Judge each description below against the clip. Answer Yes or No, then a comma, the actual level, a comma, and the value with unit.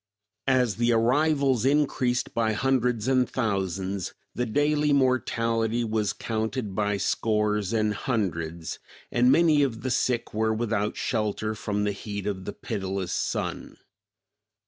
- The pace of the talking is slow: Yes, slow, 130 wpm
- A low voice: Yes, low, 115 Hz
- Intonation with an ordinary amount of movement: Yes, average, 3.6 semitones